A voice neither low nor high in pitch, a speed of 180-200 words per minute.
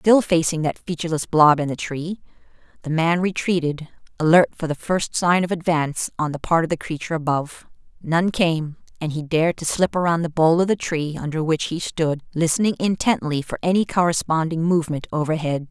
Yes: medium, 165 Hz; average, 185 wpm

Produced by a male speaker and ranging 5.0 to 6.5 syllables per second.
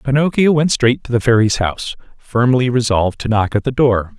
Yes: male; 5.5 syllables/s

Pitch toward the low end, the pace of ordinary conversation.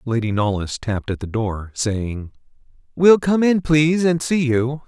Yes: low, 130 Hz; average, 160 wpm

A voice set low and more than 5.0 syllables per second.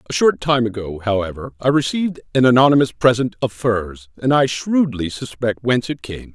Yes: low, 120 Hz; 5.3 syllables/s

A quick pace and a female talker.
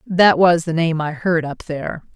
Yes: fast, 225 wpm; female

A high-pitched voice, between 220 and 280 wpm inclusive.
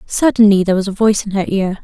Yes: high, 205 Hz; fast, 260 wpm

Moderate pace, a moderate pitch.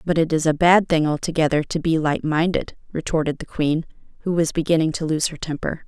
No: fast, 215 wpm; medium, 160 Hz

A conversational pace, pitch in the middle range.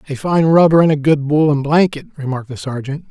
No: fast, 210 wpm; medium, 145 Hz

